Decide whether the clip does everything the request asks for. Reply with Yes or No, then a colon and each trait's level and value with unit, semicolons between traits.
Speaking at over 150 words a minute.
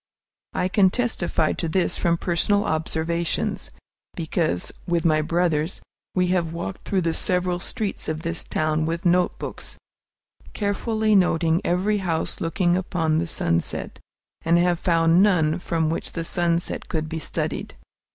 No: average, 140 wpm